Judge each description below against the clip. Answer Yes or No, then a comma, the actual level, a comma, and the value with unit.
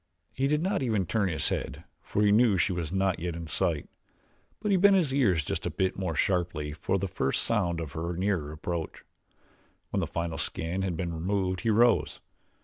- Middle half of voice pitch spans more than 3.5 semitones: Yes, average, 4.1 semitones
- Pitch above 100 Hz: No, very low, 95 Hz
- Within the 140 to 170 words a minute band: No, fast, 205 wpm